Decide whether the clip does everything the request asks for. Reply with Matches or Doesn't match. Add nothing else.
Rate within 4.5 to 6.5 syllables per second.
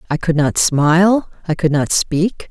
Doesn't match